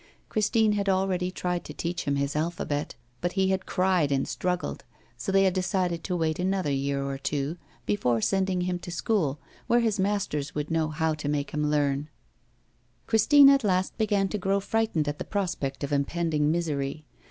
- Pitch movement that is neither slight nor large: Yes, average, 4.7 semitones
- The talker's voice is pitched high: No, medium, 175 Hz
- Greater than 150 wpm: Yes, average, 185 wpm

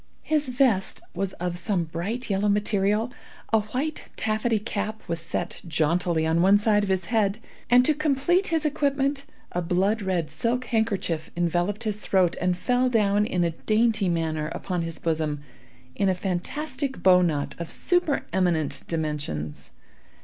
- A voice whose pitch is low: No, high, 200 Hz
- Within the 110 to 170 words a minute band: Yes, average, 155 wpm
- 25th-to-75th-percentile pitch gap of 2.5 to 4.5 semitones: No, wide, 5.5 semitones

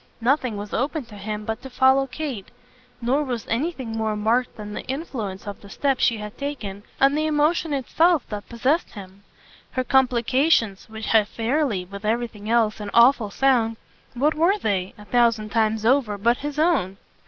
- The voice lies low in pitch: No, high, 235 Hz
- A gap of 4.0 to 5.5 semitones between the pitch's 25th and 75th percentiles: Yes, average, 4.5 semitones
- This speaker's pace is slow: No, average, 175 wpm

